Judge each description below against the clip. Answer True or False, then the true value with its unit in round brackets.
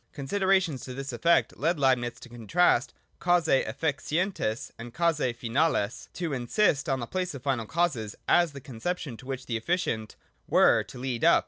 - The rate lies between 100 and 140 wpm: False (180 wpm)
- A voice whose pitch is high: False (135 Hz)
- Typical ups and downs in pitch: False (5.9 semitones)